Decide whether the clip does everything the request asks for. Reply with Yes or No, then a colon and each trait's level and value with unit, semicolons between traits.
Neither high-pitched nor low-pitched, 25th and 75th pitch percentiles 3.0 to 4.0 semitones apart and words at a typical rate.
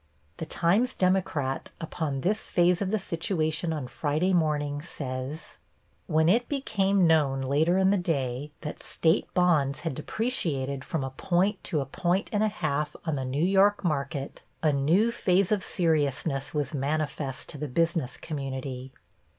No: medium, 155 Hz; average, 4.6 semitones; average, 160 wpm